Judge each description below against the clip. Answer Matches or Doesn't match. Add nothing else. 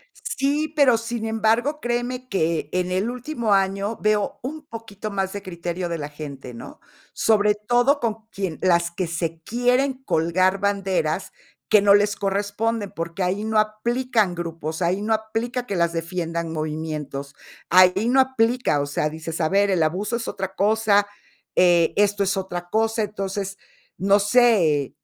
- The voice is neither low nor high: Doesn't match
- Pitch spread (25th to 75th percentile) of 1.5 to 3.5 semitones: Doesn't match